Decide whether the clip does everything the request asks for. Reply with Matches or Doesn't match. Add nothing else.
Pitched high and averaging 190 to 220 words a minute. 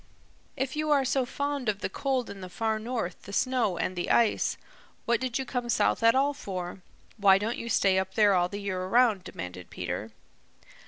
Matches